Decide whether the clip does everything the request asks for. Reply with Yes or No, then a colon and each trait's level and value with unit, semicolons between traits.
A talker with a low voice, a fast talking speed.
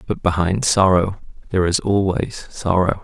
No: very low, 95 Hz; average, 140 wpm